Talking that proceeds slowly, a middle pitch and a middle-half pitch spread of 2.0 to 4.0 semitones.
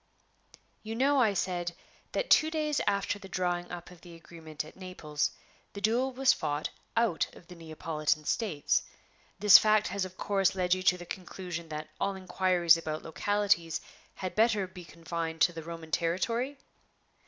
No: average, 165 wpm; medium, 180 Hz; average, 3.6 semitones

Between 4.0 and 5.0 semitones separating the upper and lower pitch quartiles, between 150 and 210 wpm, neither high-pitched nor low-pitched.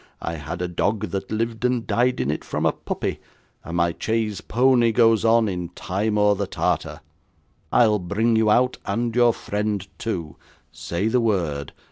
No: average, 4.3 semitones; average, 170 wpm; low, 105 Hz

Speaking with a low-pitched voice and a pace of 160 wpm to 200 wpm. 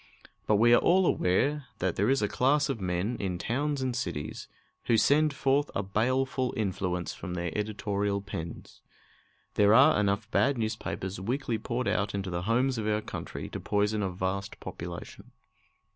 Yes: low, 105 Hz; average, 170 wpm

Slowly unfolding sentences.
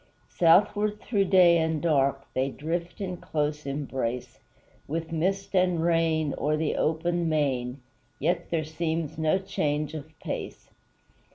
Yes: slow, 130 wpm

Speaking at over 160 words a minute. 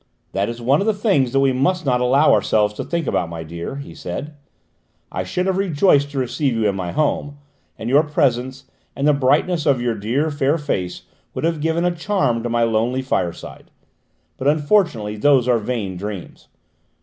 Yes: average, 195 wpm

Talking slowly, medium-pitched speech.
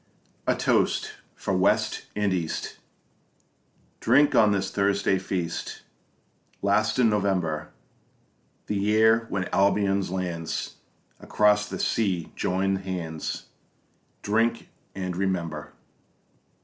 No: slow, 95 wpm; low, 100 Hz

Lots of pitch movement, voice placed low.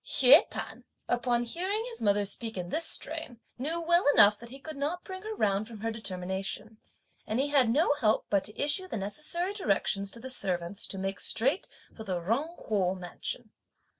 No: wide, 7.5 semitones; high, 230 Hz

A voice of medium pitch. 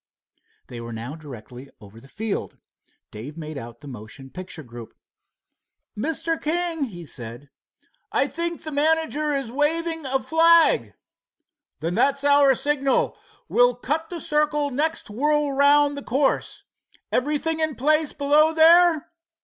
No: very high, 280 Hz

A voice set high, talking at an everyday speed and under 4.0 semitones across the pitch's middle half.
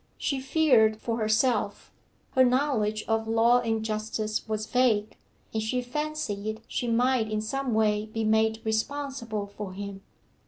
Yes: high, 220 Hz; average, 145 wpm; average, 2.7 semitones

